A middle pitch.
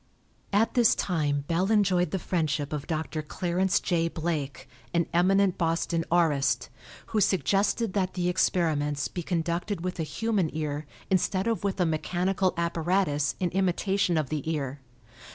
Yes: medium, 170 Hz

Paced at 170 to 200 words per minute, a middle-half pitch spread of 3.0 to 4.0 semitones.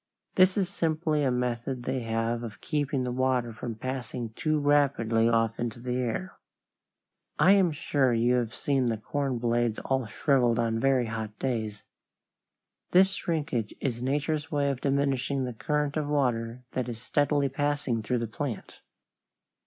No: average, 160 wpm; average, 3.7 semitones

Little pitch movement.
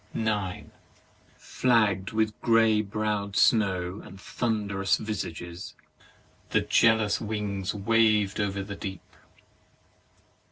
Yes: narrow, 2.1 semitones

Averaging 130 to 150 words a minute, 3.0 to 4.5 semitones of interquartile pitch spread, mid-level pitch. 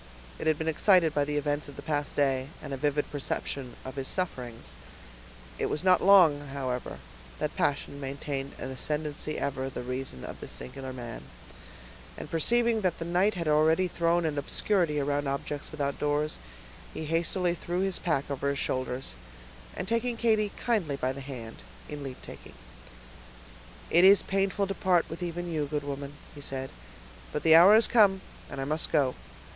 No: average, 175 wpm; average, 4.2 semitones; medium, 150 Hz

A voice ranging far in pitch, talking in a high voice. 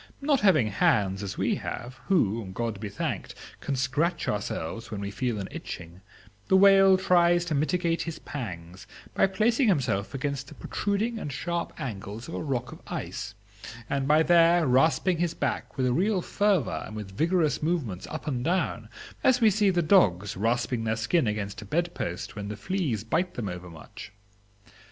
No: wide, 8.6 semitones; medium, 140 Hz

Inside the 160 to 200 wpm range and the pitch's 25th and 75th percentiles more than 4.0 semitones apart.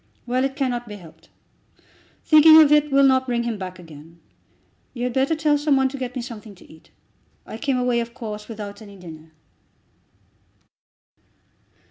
Yes: average, 170 wpm; average, 5.1 semitones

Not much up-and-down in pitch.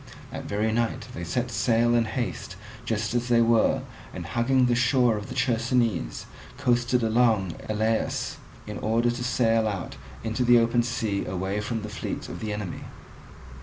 Yes: narrow, 2.1 semitones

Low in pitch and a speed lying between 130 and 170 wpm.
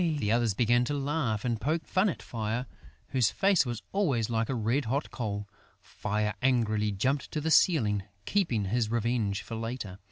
No: low, 120 Hz; average, 180 wpm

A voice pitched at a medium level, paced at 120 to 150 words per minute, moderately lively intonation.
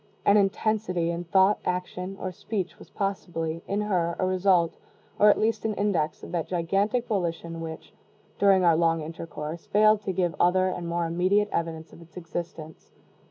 No: medium, 180 Hz; average, 170 wpm; average, 3.1 semitones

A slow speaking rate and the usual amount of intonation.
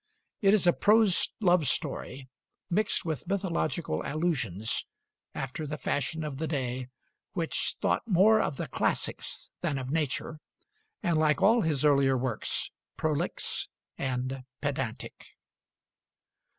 Yes: slow, 125 wpm; average, 4.7 semitones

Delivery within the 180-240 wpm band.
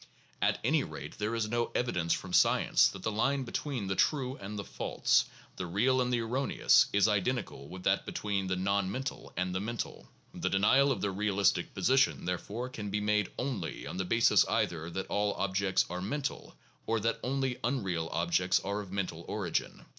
Yes: average, 190 wpm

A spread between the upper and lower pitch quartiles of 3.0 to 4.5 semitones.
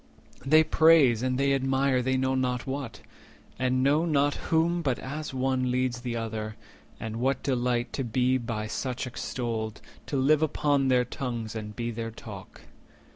No: narrow, 2.6 semitones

